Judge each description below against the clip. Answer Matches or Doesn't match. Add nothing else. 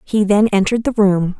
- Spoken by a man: Doesn't match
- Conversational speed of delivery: Doesn't match